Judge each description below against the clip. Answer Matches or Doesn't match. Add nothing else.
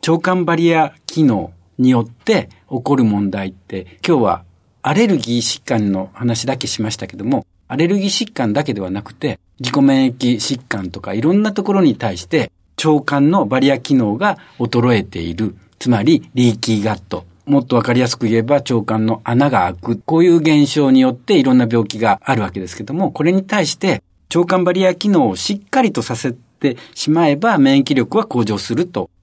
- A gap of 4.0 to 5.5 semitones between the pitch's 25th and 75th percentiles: Doesn't match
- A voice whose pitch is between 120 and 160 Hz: Matches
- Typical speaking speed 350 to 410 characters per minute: Matches